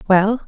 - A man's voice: No, female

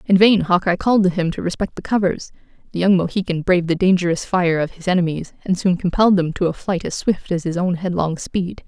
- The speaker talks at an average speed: No, fast, 235 wpm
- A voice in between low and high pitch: Yes, medium, 180 Hz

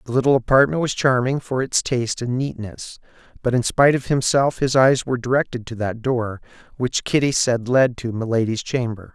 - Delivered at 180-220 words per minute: Yes, average, 190 wpm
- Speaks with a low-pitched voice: Yes, low, 125 Hz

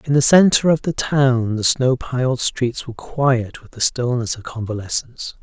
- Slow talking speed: No, average, 190 wpm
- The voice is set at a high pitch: No, low, 125 Hz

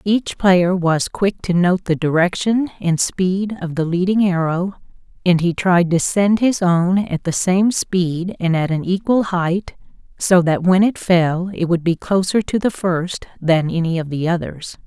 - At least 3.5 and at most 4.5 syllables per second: Yes, 4.1 syllables/s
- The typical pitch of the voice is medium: Yes, medium, 180 Hz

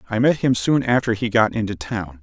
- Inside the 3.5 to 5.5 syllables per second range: Yes, 5.4 syllables/s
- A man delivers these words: Yes, male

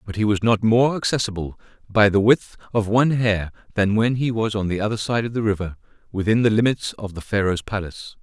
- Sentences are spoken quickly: Yes, fast, 220 wpm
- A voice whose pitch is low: Yes, low, 105 Hz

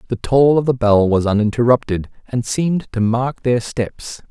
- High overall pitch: No, low, 120 Hz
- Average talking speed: Yes, average, 180 wpm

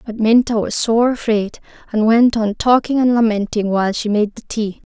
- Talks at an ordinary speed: Yes, average, 195 wpm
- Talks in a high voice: Yes, high, 220 Hz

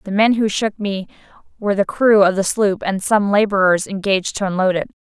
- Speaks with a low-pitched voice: No, high, 200 Hz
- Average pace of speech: No, fast, 215 wpm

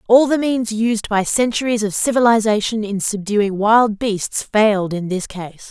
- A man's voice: No, female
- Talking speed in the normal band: Yes, average, 170 wpm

